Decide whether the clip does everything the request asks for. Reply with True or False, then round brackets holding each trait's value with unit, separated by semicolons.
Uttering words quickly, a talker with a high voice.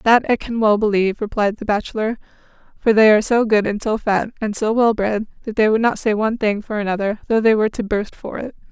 True (250 wpm; 215 Hz)